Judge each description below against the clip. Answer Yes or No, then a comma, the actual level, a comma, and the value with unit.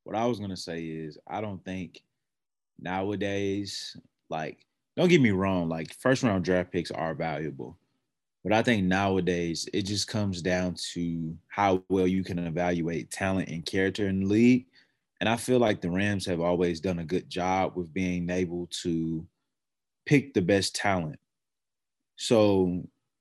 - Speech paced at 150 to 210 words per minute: Yes, average, 165 wpm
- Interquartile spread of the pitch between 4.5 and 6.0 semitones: No, narrow, 2.6 semitones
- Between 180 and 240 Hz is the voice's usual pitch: No, very low, 95 Hz